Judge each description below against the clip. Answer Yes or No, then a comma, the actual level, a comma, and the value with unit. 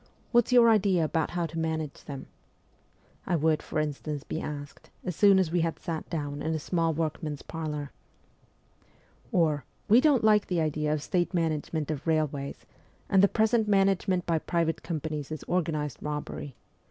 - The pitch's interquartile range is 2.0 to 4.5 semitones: Yes, average, 3.3 semitones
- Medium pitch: Yes, medium, 160 Hz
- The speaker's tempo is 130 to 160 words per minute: No, average, 175 wpm